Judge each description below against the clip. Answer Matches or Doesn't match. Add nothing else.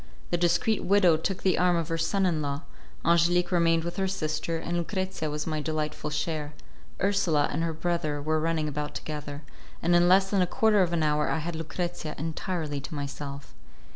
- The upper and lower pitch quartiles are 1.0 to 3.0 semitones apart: Matches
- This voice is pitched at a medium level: Matches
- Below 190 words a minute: Doesn't match